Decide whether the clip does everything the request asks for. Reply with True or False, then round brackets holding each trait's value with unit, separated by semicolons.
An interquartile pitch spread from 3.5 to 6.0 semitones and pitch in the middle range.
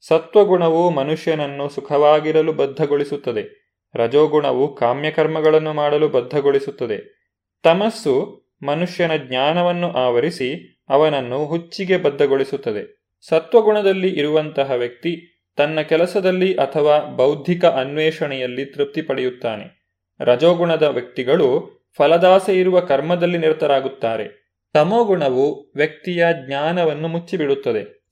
True (4.4 semitones; 160 Hz)